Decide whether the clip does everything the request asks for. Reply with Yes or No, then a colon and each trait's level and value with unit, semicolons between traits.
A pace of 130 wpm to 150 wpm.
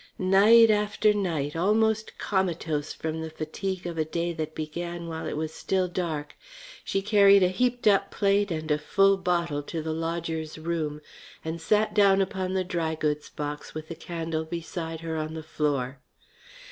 No: average, 170 wpm